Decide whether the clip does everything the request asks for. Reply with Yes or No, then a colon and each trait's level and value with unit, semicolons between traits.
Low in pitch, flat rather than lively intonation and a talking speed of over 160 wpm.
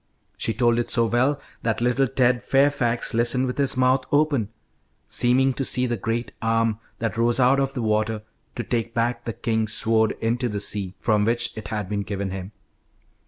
Yes: low, 120 Hz; narrow, 2.3 semitones; average, 190 wpm